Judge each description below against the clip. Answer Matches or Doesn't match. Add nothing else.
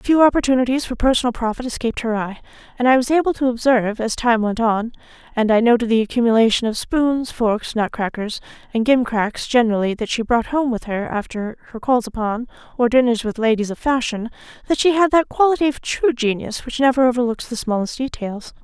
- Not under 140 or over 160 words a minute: Doesn't match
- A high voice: Matches